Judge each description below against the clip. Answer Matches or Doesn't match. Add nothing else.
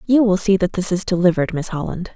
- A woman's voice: Matches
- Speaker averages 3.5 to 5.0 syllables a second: Doesn't match